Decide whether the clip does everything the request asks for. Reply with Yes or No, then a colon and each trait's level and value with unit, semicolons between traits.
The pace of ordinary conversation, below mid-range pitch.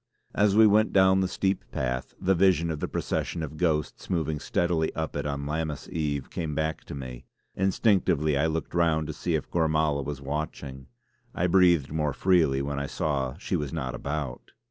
Yes: average, 190 wpm; very low, 80 Hz